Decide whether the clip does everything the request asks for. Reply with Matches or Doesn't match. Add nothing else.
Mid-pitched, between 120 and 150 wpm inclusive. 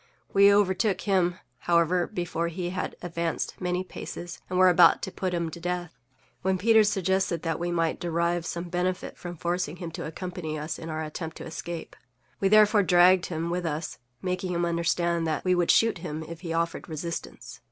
Doesn't match